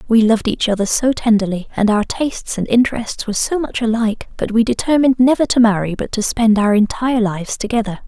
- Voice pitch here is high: Yes, high, 225 Hz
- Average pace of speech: No, fast, 210 wpm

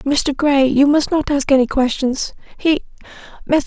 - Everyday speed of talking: Yes, average, 145 wpm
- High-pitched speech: Yes, very high, 280 Hz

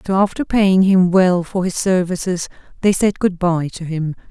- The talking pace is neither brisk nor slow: Yes, average, 195 wpm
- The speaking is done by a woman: Yes, female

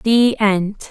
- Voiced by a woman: Yes, female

